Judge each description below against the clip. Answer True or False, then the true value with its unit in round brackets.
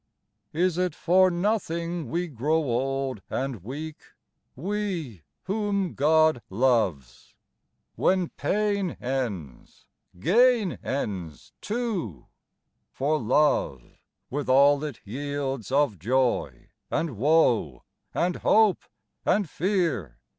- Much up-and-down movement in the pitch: True (6.7 semitones)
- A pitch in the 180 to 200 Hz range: False (145 Hz)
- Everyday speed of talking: False (95 wpm)